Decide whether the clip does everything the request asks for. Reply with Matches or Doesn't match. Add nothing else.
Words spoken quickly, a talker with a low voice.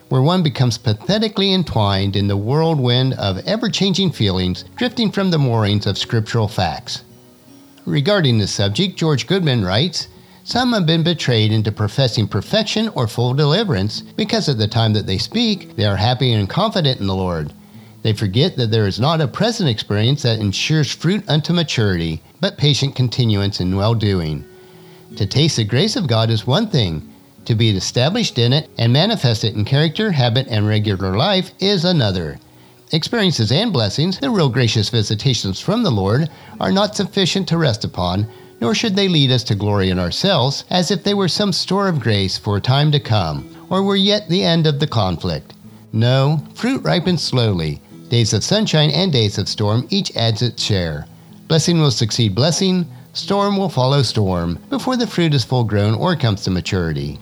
Doesn't match